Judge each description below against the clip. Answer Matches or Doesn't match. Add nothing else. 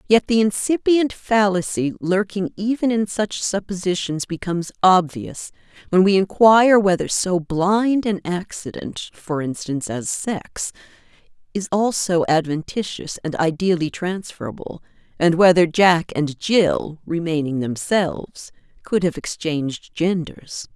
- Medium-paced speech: Doesn't match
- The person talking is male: Doesn't match